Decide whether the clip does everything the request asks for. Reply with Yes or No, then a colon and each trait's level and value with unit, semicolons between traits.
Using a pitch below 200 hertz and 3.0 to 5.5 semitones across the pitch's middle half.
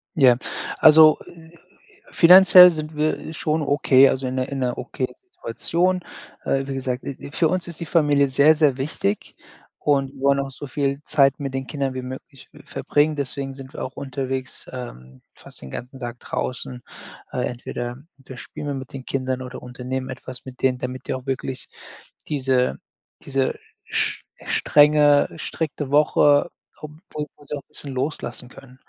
No: low, 135 Hz; narrow, 2.5 semitones